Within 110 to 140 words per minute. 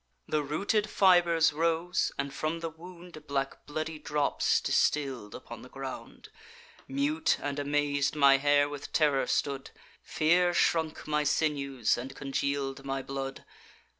Yes: slow, 135 wpm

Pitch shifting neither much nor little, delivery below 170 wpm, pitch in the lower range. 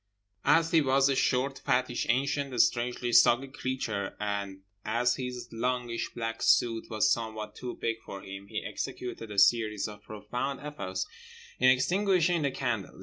Yes: average, 3.6 semitones; average, 150 wpm; low, 120 Hz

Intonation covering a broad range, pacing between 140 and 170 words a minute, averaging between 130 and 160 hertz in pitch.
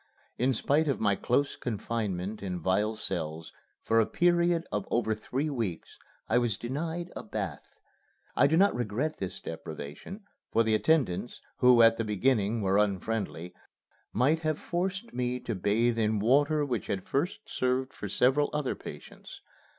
No: wide, 5.8 semitones; average, 160 wpm; low, 120 Hz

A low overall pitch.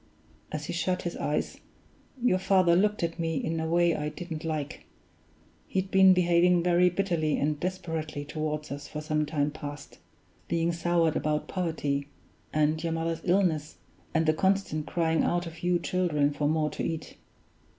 No: medium, 165 Hz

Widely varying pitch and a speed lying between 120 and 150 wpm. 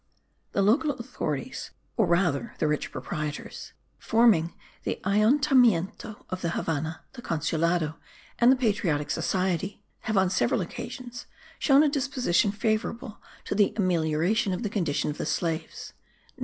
Yes: wide, 6.0 semitones; slow, 135 wpm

